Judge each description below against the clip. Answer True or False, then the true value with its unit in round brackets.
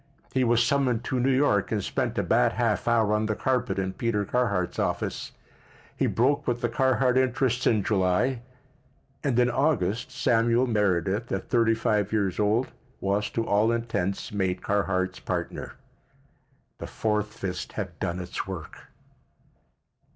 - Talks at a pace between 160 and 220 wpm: False (150 wpm)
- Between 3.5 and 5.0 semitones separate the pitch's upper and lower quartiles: True (4.0 semitones)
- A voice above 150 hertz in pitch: False (110 Hz)